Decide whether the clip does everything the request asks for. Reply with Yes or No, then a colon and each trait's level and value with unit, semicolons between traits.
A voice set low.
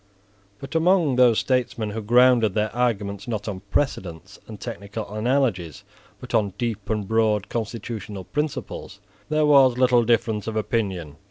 Yes: low, 110 Hz